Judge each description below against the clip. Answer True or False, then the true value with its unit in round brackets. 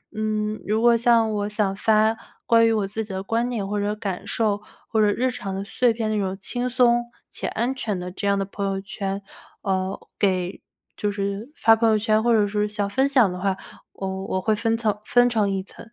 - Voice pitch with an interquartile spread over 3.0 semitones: False (2.4 semitones)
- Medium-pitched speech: False (210 Hz)